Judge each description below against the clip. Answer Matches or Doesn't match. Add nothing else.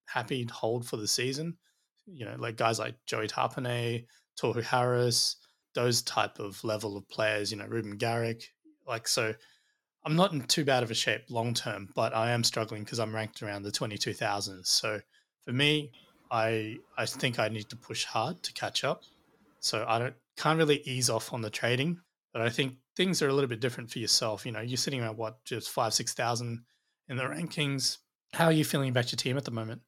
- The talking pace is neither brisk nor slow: Doesn't match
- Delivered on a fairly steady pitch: Doesn't match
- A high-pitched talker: Doesn't match